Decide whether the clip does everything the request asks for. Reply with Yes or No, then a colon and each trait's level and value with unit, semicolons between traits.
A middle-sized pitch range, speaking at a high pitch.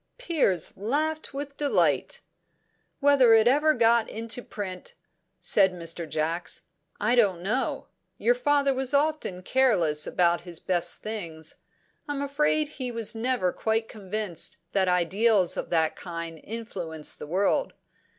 No: wide, 7.1 semitones; high, 220 Hz